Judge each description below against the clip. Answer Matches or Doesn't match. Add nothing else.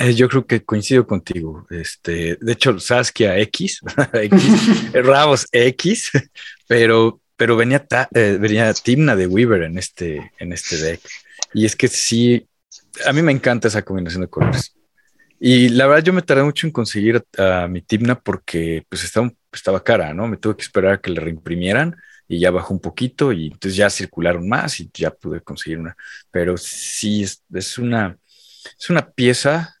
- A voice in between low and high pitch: Doesn't match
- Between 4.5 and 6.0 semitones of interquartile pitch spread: Matches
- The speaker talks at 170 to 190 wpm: Matches